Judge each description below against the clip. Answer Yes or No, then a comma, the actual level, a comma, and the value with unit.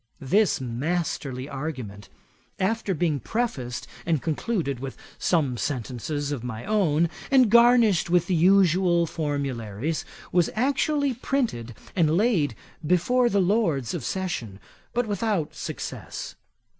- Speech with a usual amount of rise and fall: No, wide, 7.3 semitones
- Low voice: No, medium, 170 Hz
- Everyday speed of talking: No, slow, 120 wpm